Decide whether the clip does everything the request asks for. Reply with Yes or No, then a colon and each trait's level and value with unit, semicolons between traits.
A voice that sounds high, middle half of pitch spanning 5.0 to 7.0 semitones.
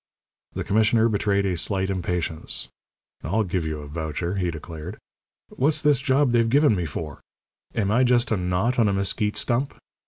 No: low, 100 Hz; average, 5.3 semitones